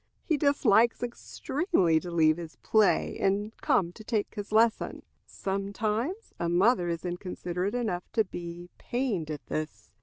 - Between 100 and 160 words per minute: Yes, average, 145 wpm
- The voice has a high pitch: Yes, high, 200 Hz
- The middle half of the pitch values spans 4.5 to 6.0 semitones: Yes, average, 5.0 semitones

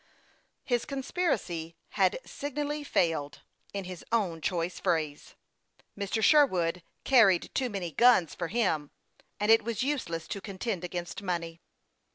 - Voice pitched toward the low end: No, high, 190 Hz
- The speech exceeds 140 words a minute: No, slow, 135 wpm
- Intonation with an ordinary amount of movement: No, wide, 6.0 semitones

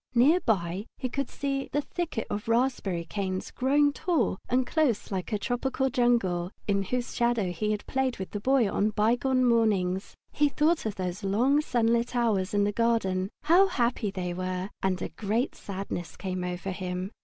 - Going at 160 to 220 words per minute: Yes, average, 180 wpm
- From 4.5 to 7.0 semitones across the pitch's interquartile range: Yes, average, 5.2 semitones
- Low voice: No, high, 220 Hz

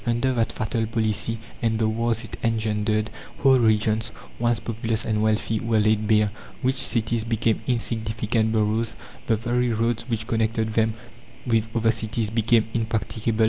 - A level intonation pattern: Yes, narrow, 1.1 semitones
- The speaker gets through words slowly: No, average, 150 wpm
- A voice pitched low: Yes, low, 110 Hz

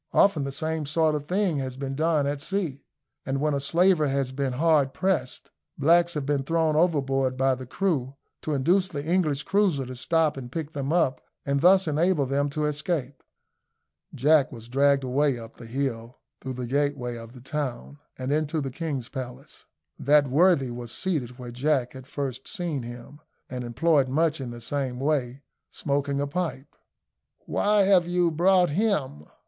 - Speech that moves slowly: No, average, 175 wpm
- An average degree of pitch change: Yes, average, 3.6 semitones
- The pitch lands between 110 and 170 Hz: Yes, medium, 140 Hz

